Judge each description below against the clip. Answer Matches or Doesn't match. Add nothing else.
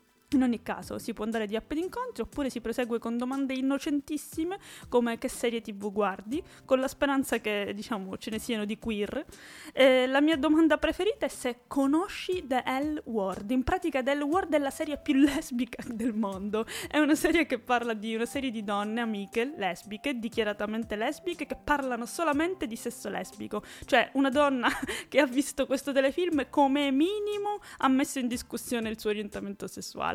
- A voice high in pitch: Matches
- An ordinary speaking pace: Doesn't match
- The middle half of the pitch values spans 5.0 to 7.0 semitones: Doesn't match